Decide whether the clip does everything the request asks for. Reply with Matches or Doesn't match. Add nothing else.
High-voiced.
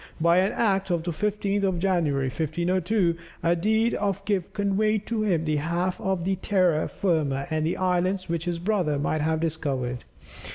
Doesn't match